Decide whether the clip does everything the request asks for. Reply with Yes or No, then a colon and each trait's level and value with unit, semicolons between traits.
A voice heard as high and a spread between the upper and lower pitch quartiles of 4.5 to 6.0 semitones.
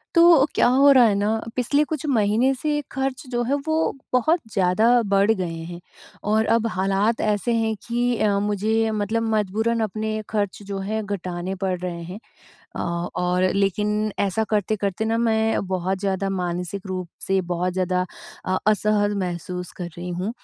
No: high, 205 Hz; average, 3.1 semitones